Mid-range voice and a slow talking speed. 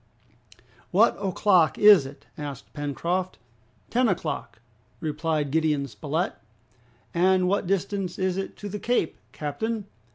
Yes: medium, 175 Hz; slow, 120 wpm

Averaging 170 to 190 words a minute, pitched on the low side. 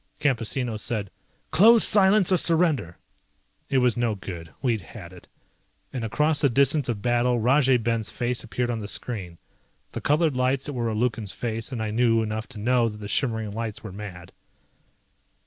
Yes: average, 180 wpm; low, 120 Hz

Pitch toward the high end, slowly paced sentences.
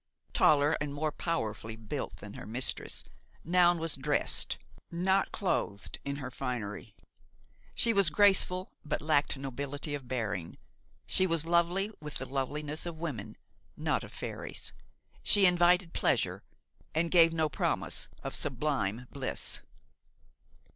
No: medium, 150 Hz; slow, 130 wpm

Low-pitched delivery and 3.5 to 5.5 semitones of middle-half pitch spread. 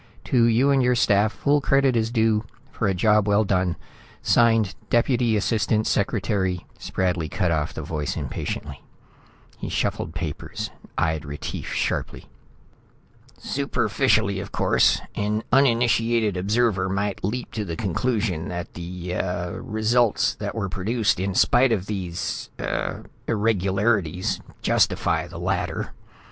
Yes: low, 105 Hz; average, 4.1 semitones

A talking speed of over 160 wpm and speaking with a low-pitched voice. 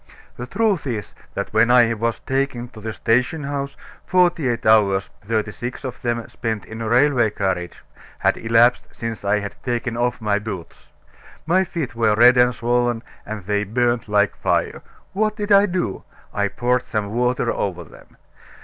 Yes: average, 175 wpm; low, 120 Hz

